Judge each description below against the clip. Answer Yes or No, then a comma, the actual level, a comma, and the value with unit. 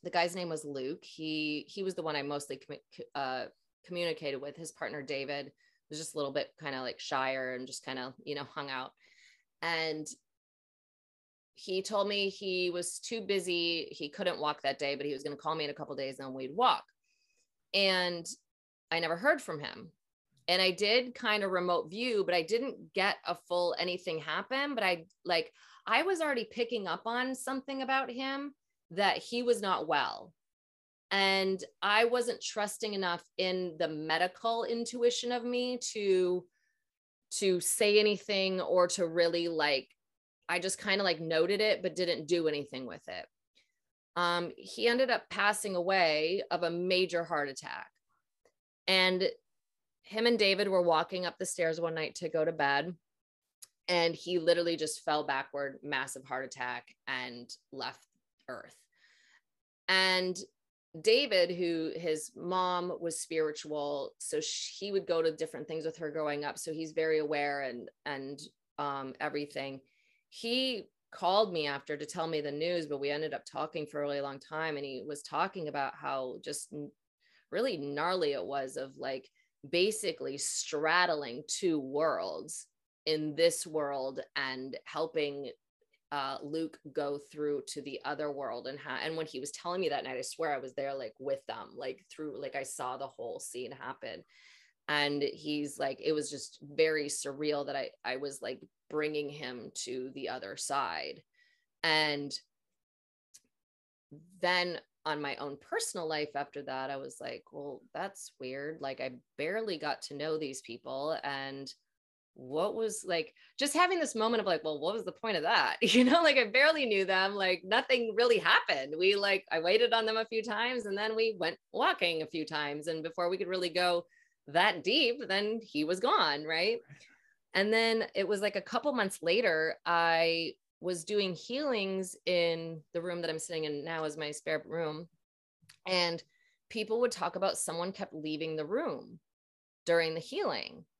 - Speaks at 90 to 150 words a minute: No, average, 175 wpm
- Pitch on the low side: No, medium, 170 Hz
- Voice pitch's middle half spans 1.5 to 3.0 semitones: No, wide, 5.5 semitones